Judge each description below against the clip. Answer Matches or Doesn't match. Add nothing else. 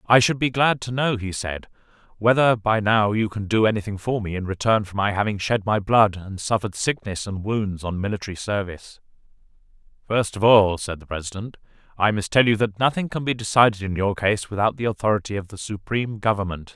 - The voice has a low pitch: Matches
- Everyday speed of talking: Doesn't match